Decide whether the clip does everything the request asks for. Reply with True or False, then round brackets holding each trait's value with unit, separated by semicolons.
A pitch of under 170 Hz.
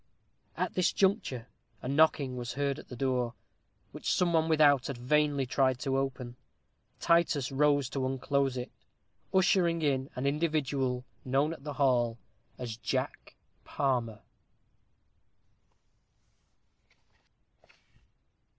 True (135 Hz)